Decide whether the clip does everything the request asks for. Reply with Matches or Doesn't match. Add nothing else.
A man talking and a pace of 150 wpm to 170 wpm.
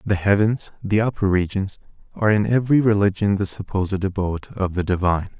Matches